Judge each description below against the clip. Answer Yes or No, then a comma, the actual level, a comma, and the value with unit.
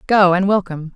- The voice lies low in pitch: No, medium, 185 Hz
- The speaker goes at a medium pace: Yes, average, 190 wpm